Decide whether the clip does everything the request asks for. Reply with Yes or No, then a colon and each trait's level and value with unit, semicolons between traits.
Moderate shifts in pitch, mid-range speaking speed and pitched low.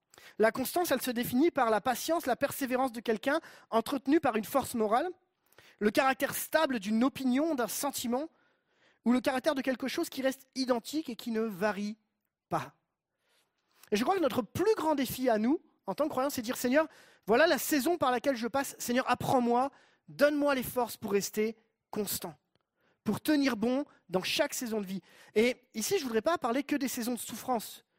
No: average, 4.0 semitones; average, 195 wpm; very high, 255 Hz